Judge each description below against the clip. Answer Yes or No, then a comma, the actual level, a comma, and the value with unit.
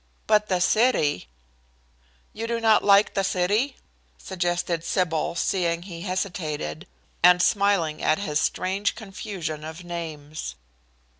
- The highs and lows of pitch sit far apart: No, average, 3.7 semitones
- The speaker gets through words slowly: Yes, slow, 120 wpm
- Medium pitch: Yes, medium, 180 Hz